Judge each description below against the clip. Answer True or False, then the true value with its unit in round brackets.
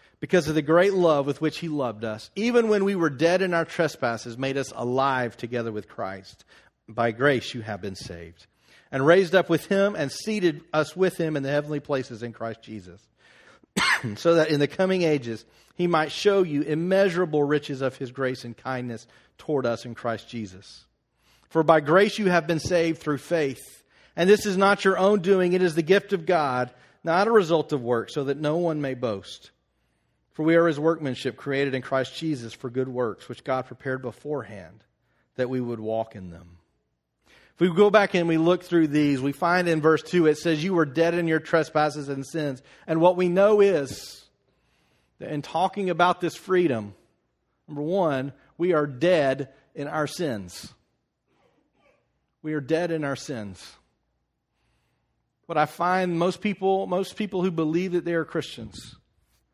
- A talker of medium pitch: True (150 Hz)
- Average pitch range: False (5.8 semitones)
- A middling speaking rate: True (185 wpm)